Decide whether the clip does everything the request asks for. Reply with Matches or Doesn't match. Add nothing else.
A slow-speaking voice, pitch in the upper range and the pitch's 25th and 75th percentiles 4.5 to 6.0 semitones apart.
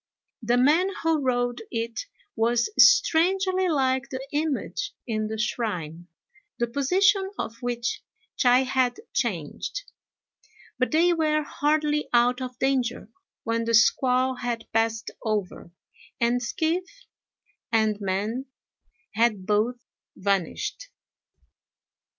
Matches